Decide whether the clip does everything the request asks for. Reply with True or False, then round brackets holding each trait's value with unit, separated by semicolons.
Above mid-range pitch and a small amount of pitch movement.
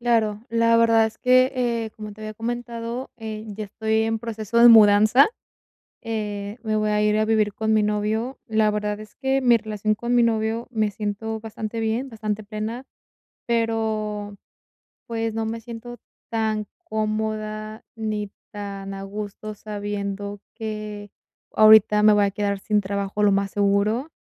True (215 Hz; 1.4 semitones)